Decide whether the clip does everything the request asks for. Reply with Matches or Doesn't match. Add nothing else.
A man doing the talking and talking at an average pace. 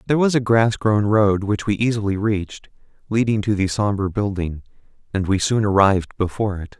Matches